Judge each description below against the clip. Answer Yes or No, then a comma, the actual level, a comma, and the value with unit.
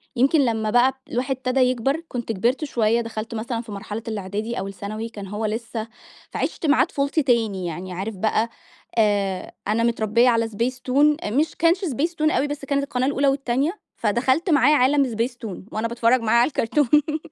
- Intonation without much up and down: No, average, 4.0 semitones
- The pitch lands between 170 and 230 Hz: No, high, 240 Hz